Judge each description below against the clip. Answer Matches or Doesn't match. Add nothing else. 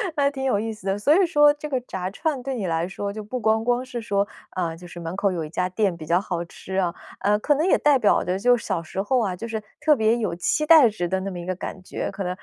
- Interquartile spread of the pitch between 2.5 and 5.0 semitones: Doesn't match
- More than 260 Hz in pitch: Doesn't match